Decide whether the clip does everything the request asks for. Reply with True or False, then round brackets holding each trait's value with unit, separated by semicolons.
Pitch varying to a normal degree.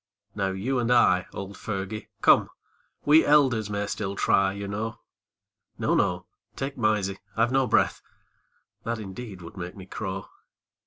True (3.6 semitones)